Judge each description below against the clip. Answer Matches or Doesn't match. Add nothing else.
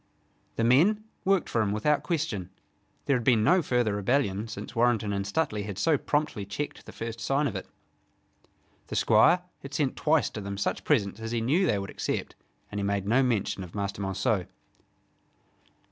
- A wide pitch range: Matches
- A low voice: Matches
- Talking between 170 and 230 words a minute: Matches